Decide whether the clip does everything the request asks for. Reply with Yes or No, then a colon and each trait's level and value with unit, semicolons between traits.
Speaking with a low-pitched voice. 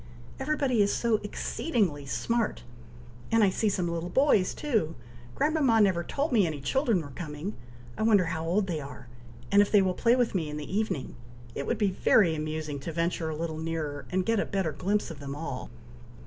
No: medium, 185 Hz